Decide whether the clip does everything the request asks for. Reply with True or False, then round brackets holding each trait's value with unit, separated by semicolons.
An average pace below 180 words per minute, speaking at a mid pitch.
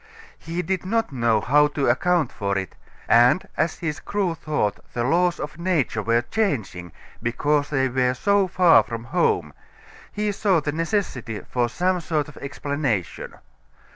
True (155 wpm; 150 Hz)